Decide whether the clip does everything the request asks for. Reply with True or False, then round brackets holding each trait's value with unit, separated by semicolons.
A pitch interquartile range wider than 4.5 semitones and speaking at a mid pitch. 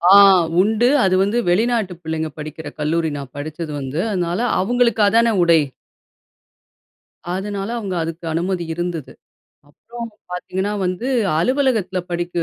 True (5.0 semitones; 180 Hz)